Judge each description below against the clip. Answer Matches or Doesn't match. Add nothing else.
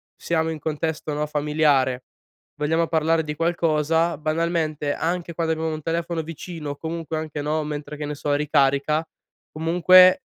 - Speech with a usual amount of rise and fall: Doesn't match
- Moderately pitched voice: Matches